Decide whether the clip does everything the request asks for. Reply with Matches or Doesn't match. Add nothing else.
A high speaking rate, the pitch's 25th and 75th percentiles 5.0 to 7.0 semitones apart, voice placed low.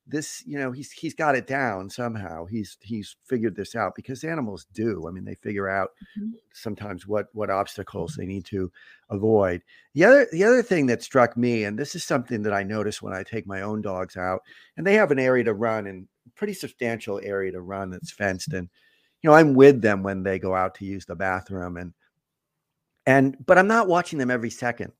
Matches